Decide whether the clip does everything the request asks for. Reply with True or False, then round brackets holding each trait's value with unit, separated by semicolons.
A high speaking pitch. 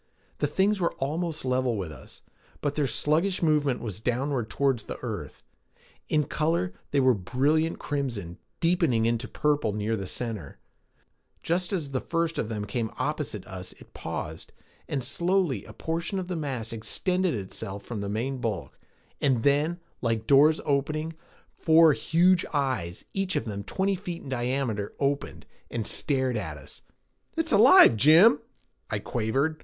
False (135 Hz)